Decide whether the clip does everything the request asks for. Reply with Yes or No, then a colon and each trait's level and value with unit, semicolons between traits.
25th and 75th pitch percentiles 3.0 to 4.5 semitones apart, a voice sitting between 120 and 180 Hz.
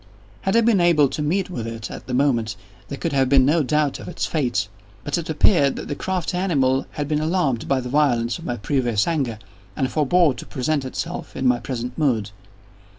Yes: average, 4.2 semitones; medium, 140 Hz